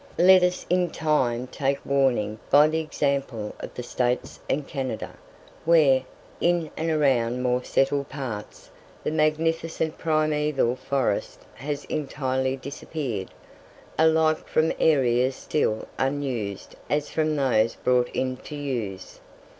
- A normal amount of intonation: Yes, average, 3.6 semitones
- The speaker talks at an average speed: No, slow, 125 wpm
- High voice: No, medium, 140 Hz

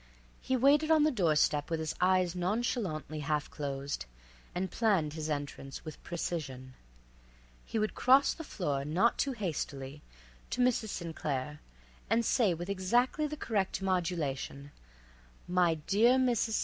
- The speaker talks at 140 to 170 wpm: Yes, average, 150 wpm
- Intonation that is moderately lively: No, wide, 7.4 semitones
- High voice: No, medium, 180 Hz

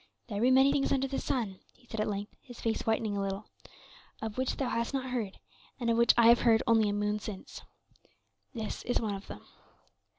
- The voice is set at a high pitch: Yes, high, 230 Hz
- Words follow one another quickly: Yes, fast, 220 wpm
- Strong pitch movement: No, average, 3.2 semitones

